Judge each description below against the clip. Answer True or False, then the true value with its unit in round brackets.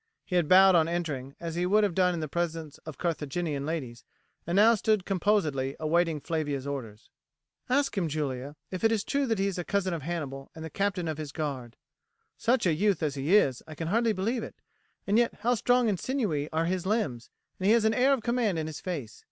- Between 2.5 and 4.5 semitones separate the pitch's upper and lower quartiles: False (5.5 semitones)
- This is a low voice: False (170 Hz)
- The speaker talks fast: True (225 wpm)